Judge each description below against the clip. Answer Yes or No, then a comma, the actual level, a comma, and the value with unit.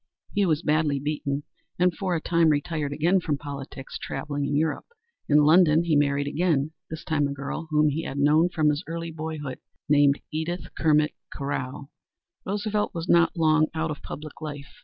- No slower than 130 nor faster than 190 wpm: Yes, average, 180 wpm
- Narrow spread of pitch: Yes, narrow, 2.3 semitones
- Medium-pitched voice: Yes, medium, 155 Hz